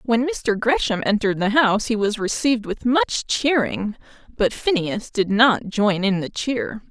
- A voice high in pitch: Yes, high, 225 Hz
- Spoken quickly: No, average, 175 wpm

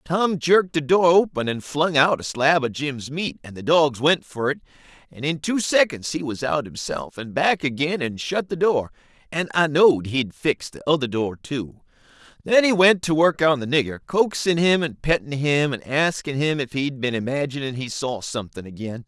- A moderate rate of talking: No, fast, 210 wpm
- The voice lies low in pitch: No, medium, 145 Hz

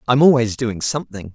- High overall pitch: No, low, 120 Hz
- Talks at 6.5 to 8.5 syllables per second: No, 5.9 syllables/s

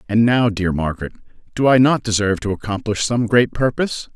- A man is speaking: Yes, male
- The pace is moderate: Yes, average, 190 wpm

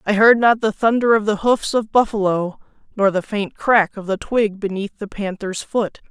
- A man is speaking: No, female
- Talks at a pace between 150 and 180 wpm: No, fast, 205 wpm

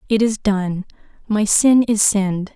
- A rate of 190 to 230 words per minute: No, average, 140 wpm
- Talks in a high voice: Yes, high, 205 Hz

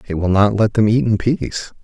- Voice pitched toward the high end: No, low, 105 Hz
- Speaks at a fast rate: Yes, fast, 260 wpm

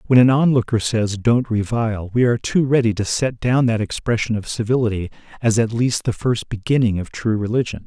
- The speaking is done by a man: Yes, male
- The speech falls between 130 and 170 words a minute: No, average, 200 wpm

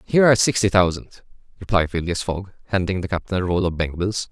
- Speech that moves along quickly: Yes, fast, 210 wpm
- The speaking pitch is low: Yes, very low, 95 Hz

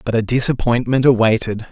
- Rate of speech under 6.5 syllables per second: Yes, 5.7 syllables/s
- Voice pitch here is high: No, low, 120 Hz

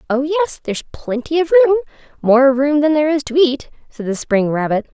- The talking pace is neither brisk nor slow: Yes, average, 190 wpm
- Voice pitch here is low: No, very high, 285 Hz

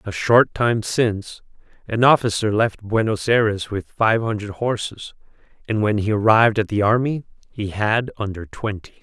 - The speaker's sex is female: No, male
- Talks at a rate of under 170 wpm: Yes, average, 160 wpm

